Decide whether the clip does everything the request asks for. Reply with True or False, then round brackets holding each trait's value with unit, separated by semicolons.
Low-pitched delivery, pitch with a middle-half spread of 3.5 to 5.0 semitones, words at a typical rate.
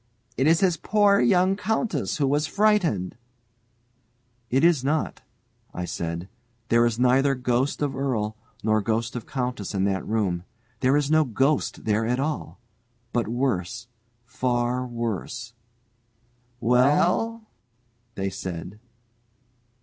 False (125 Hz; 4.7 semitones; 130 wpm)